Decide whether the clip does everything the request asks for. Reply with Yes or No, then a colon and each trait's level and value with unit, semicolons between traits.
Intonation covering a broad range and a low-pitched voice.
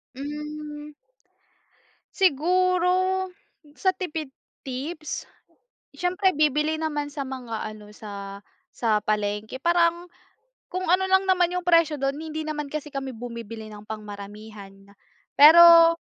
No: wide, 7.0 semitones; very high, 300 Hz